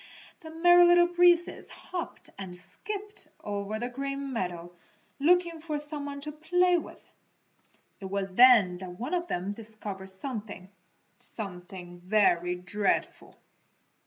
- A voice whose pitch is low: No, high, 230 Hz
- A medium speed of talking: No, slow, 130 wpm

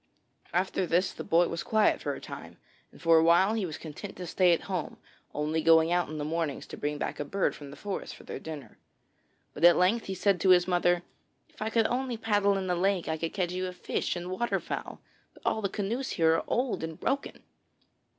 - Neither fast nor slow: No, fast, 230 wpm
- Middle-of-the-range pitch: Yes, medium, 180 Hz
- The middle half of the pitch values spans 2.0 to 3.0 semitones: No, average, 3.5 semitones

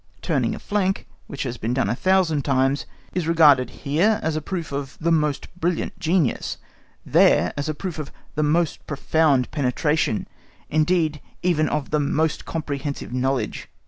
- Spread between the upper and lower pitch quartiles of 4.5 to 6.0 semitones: No, average, 3.1 semitones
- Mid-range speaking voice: Yes, medium, 150 Hz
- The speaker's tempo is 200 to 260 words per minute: No, average, 160 wpm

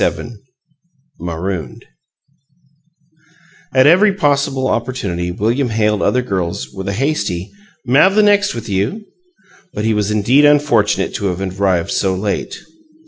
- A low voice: Yes, low, 105 Hz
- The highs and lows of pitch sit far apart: Yes, wide, 6.1 semitones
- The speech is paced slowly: Yes, slow, 125 wpm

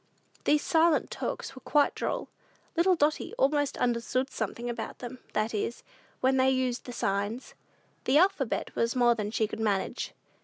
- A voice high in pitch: Yes, very high, 255 Hz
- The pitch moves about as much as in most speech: Yes, average, 4.0 semitones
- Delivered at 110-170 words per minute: Yes, average, 160 wpm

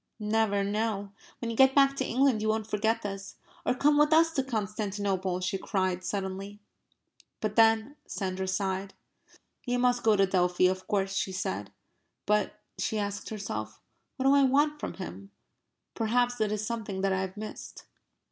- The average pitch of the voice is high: Yes, high, 210 Hz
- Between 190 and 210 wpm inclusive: No, average, 170 wpm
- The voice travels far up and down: No, average, 3.4 semitones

